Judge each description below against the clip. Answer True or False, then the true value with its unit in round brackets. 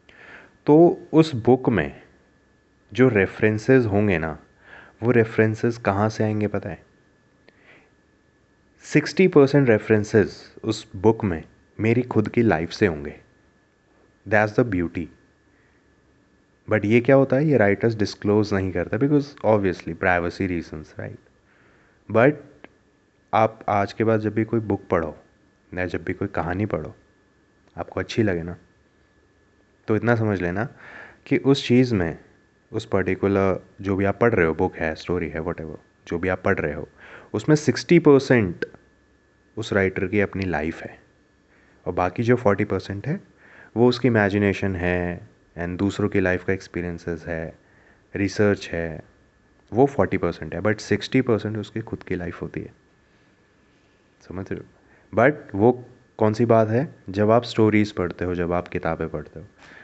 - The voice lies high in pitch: False (100 Hz)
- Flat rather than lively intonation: False (3.8 semitones)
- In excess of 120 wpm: True (150 wpm)